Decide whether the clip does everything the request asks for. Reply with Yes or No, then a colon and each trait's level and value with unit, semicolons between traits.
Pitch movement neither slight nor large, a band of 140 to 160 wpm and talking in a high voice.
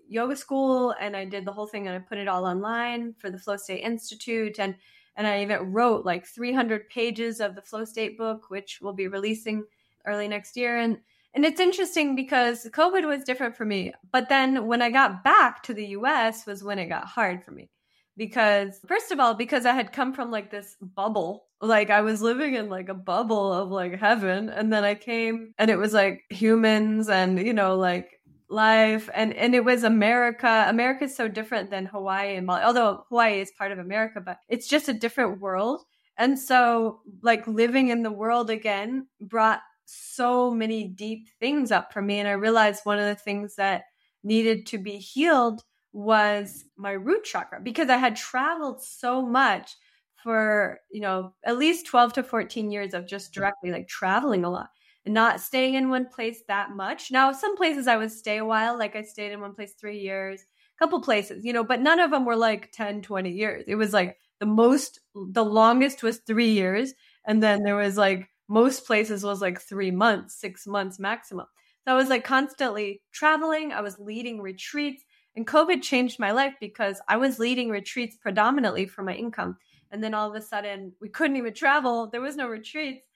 No: average, 3.3 semitones; fast, 205 wpm; high, 220 Hz